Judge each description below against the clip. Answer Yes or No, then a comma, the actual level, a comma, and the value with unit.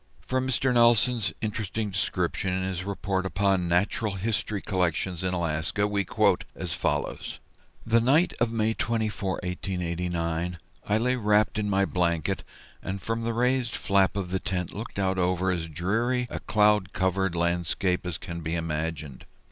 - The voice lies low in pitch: Yes, very low, 95 Hz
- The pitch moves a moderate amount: Yes, average, 3.6 semitones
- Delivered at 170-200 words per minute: No, average, 155 wpm